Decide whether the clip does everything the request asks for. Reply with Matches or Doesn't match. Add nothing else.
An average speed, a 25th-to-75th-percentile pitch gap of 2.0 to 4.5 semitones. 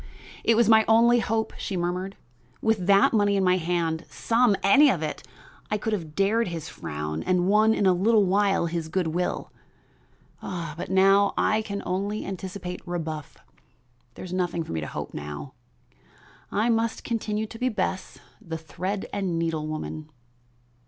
Matches